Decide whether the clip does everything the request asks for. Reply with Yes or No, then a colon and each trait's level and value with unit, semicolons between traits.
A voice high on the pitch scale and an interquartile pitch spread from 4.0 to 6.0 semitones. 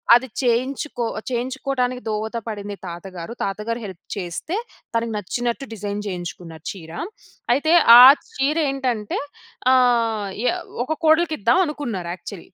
Yes: high, 235 Hz; average, 4.7 semitones